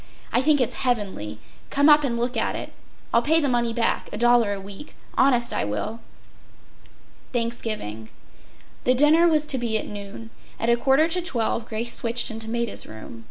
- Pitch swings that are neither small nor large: Yes, average, 3.5 semitones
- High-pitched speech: Yes, high, 235 Hz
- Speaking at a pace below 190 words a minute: Yes, average, 175 wpm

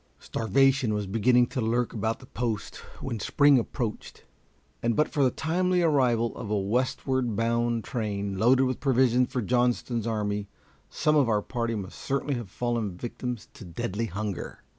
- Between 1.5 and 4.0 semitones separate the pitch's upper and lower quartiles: Yes, average, 3.1 semitones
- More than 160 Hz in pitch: No, low, 120 Hz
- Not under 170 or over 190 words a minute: No, average, 160 wpm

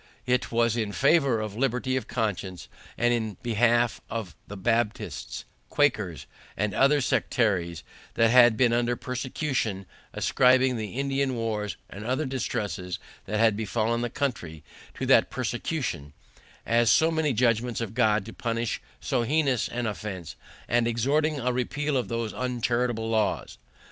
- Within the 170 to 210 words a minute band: No, average, 145 wpm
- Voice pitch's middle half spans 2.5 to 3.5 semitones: Yes, average, 2.9 semitones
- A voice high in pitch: No, low, 115 Hz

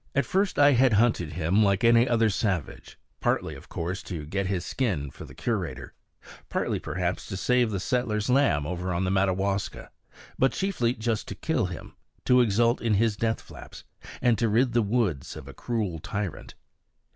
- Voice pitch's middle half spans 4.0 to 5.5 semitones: Yes, average, 4.6 semitones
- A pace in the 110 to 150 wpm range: No, average, 180 wpm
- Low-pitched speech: Yes, low, 105 Hz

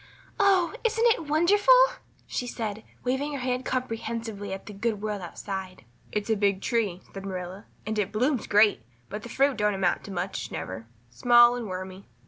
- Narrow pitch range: No, average, 4.6 semitones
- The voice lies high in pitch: Yes, high, 215 Hz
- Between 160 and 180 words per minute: Yes, average, 175 wpm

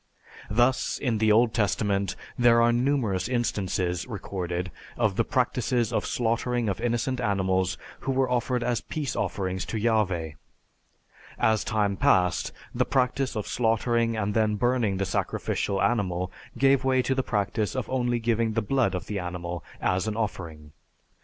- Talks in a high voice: No, low, 110 Hz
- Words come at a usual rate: Yes, average, 155 wpm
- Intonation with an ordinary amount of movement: Yes, average, 4.0 semitones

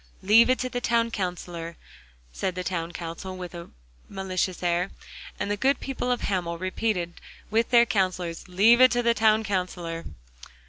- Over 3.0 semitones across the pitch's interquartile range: Yes, average, 4.6 semitones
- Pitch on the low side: No, high, 190 Hz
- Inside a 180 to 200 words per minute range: No, average, 170 wpm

